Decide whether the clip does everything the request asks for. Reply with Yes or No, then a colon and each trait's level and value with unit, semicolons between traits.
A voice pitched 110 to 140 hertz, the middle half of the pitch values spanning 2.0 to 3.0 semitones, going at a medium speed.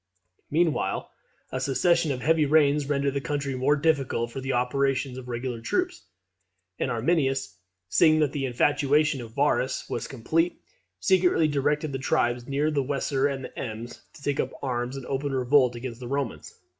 Yes: low, 135 Hz; narrow, 2.6 semitones; average, 170 wpm